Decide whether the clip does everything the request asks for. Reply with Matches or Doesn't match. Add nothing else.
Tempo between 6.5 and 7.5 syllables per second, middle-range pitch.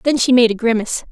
Doesn't match